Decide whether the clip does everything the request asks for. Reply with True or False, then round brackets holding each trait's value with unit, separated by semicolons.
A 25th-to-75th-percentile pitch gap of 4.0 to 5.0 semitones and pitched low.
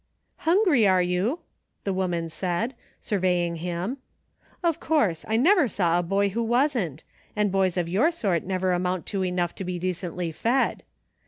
False (4.6 semitones; 185 Hz)